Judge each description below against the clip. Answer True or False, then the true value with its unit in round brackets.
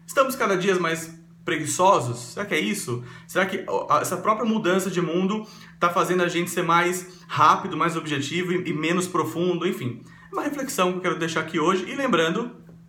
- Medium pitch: True (175 Hz)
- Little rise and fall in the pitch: True (2.3 semitones)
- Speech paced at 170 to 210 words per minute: True (185 wpm)